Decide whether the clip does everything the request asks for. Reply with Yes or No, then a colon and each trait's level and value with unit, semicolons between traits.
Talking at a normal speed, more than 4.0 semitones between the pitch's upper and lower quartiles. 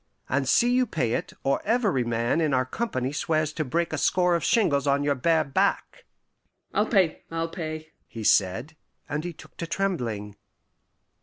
Yes: average, 175 wpm; average, 5.3 semitones